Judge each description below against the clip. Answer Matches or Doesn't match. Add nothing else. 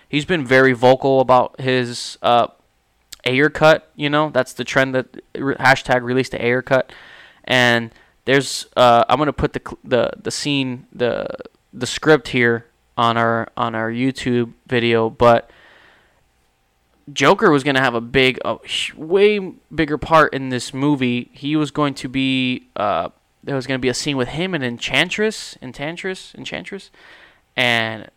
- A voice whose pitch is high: Doesn't match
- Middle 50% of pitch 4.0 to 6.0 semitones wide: Doesn't match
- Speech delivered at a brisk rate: Doesn't match